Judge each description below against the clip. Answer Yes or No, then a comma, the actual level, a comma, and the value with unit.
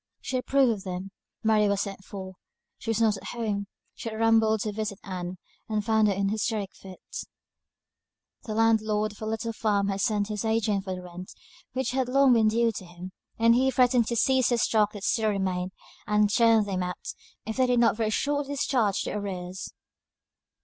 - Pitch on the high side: Yes, high, 215 Hz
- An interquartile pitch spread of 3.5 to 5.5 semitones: No, narrow, 2.5 semitones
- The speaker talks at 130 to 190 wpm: No, average, 200 wpm